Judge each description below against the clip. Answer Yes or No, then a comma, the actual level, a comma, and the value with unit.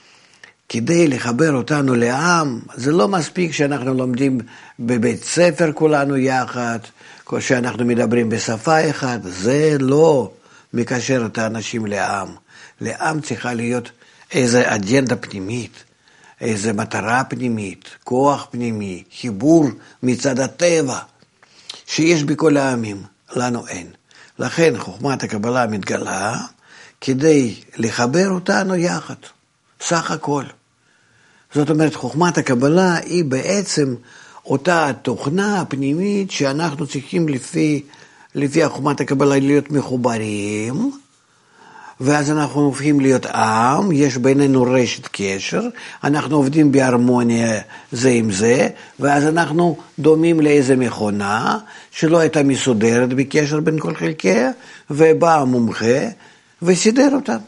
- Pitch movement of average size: Yes, average, 4.6 semitones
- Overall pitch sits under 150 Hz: Yes, medium, 140 Hz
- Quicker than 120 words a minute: No, average, 105 wpm